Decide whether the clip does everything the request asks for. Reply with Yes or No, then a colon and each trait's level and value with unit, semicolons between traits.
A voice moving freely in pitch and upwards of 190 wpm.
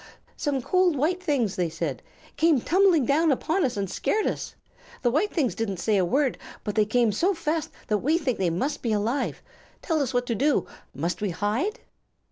Yes: wide, 7.4 semitones; average, 200 wpm